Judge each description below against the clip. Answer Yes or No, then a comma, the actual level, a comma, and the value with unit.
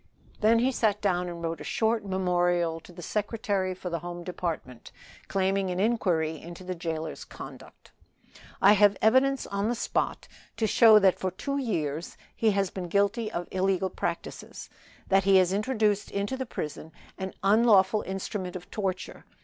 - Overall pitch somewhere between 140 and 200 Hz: Yes, high, 190 Hz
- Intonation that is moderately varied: Yes, average, 3.3 semitones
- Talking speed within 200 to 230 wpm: No, average, 165 wpm